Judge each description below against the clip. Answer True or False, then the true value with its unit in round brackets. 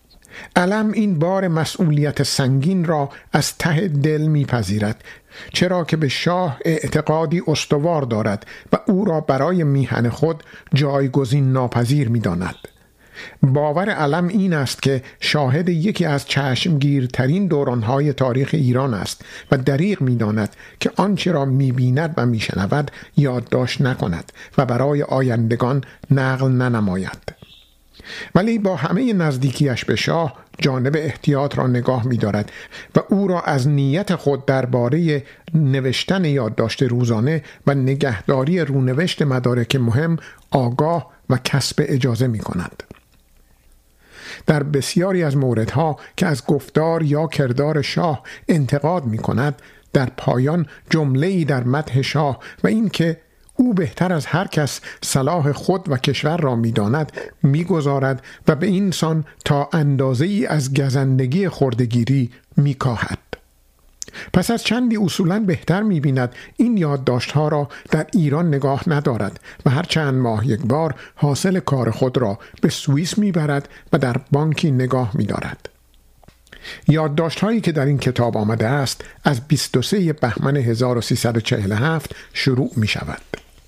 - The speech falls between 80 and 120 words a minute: False (130 wpm)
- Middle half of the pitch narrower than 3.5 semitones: False (4.4 semitones)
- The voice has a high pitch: False (140 Hz)